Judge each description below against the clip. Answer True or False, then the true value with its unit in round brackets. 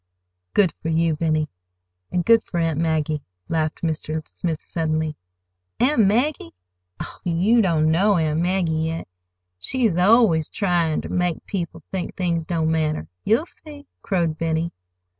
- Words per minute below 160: True (140 wpm)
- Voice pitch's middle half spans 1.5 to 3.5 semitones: True (3.1 semitones)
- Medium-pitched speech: True (165 Hz)